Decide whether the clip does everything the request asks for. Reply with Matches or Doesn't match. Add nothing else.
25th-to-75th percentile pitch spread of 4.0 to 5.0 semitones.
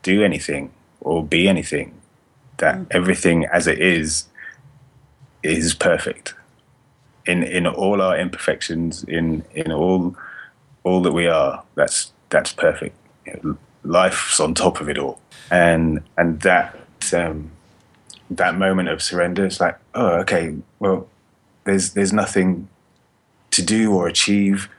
Doesn't match